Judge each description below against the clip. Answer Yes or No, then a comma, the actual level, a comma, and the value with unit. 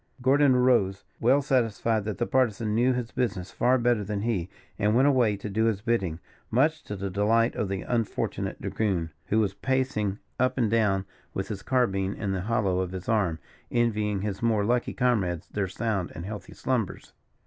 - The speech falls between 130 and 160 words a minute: No, average, 185 wpm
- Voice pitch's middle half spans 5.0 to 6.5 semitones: No, average, 3.7 semitones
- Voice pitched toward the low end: Yes, low, 110 Hz